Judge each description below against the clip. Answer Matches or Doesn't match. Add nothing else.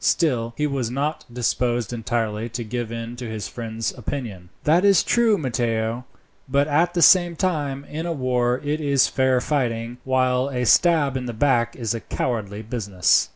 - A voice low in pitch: Matches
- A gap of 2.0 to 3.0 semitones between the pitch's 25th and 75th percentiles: Doesn't match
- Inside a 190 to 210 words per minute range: Doesn't match